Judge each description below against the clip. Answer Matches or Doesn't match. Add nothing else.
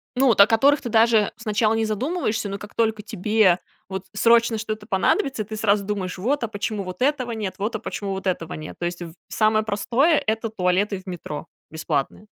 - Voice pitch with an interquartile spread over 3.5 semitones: Doesn't match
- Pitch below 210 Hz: Doesn't match